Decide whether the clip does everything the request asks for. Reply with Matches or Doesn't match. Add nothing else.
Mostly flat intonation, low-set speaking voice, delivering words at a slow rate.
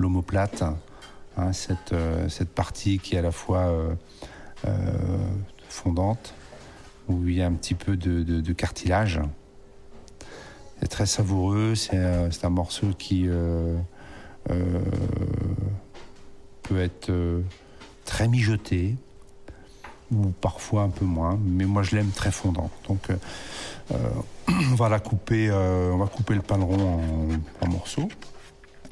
Matches